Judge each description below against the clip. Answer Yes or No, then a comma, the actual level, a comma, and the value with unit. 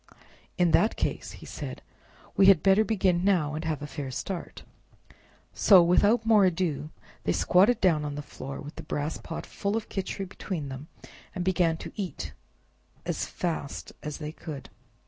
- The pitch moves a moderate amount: Yes, average, 4.4 semitones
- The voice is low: No, medium, 175 Hz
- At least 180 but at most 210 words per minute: No, average, 170 wpm